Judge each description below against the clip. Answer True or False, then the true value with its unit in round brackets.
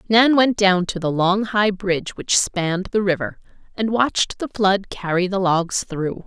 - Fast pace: False (190 wpm)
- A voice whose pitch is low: False (195 Hz)